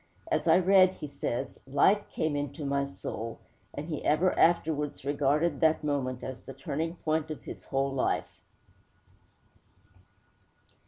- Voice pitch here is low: No, medium, 145 Hz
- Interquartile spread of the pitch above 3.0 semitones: No, average, 2.7 semitones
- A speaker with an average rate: Yes, average, 145 wpm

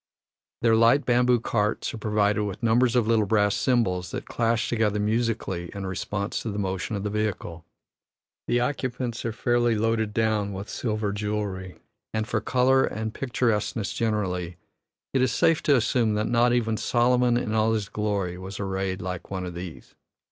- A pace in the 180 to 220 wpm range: No, average, 170 wpm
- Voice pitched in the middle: No, low, 110 Hz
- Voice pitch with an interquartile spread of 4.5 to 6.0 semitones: No, average, 3.0 semitones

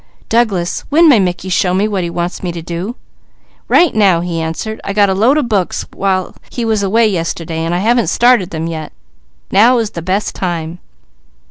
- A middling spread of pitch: Yes, average, 4.3 semitones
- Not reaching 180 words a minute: No, average, 200 wpm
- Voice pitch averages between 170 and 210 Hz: Yes, high, 190 Hz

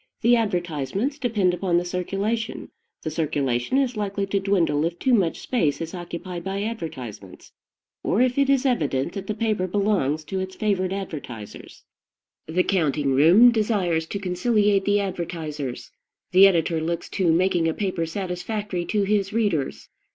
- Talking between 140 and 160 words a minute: Yes, average, 155 wpm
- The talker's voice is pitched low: No, medium, 185 Hz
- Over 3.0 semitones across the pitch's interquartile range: Yes, average, 4.1 semitones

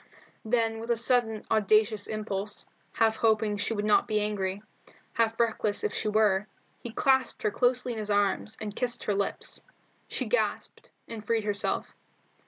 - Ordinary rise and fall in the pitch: No, narrow, 1.7 semitones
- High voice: Yes, high, 215 Hz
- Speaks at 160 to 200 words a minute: Yes, average, 165 wpm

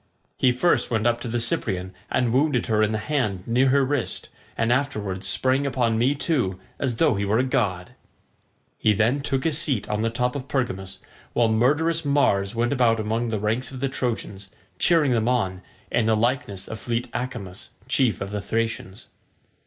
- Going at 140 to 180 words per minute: No, average, 190 wpm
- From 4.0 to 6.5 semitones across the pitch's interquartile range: No, average, 3.5 semitones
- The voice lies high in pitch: No, low, 120 Hz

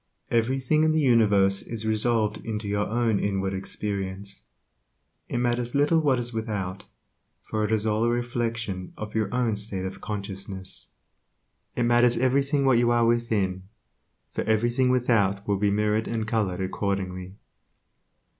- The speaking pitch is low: Yes, low, 110 Hz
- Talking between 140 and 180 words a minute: Yes, average, 145 wpm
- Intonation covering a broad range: No, average, 3.3 semitones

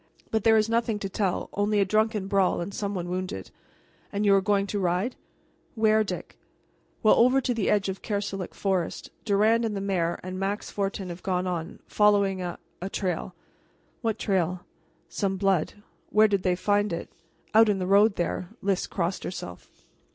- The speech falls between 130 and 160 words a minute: No, average, 180 wpm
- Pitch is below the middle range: No, high, 195 Hz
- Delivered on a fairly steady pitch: Yes, narrow, 2.3 semitones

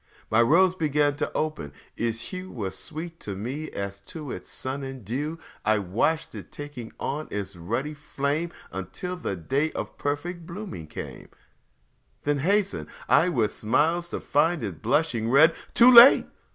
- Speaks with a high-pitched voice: No, medium, 145 Hz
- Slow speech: No, average, 165 wpm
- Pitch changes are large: Yes, wide, 6.7 semitones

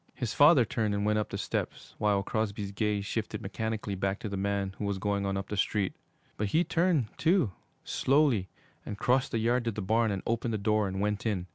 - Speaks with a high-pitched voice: No, low, 105 Hz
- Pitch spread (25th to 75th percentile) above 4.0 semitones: No, narrow, 2.6 semitones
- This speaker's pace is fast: Yes, fast, 225 wpm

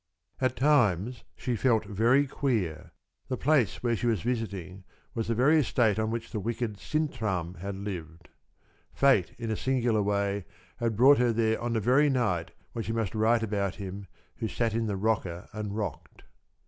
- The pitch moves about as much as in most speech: Yes, average, 3.4 semitones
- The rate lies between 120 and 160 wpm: No, average, 175 wpm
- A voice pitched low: Yes, low, 110 Hz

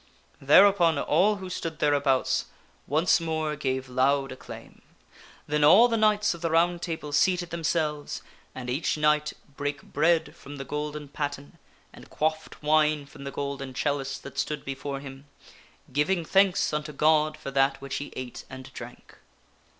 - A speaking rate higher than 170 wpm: No, average, 155 wpm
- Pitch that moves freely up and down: No, average, 2.8 semitones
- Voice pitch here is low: No, medium, 150 Hz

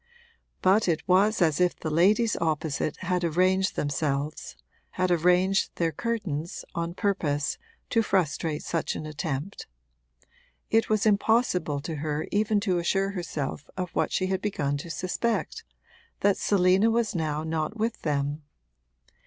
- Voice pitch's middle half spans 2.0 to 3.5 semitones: No, average, 4.4 semitones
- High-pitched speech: No, medium, 180 Hz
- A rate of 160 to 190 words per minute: No, average, 140 wpm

